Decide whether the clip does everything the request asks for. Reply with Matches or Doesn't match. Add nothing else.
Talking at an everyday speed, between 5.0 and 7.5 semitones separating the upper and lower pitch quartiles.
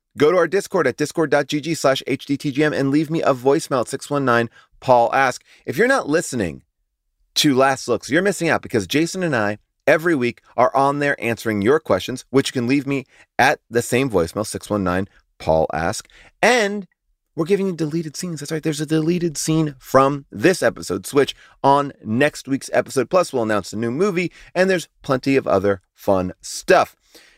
Matches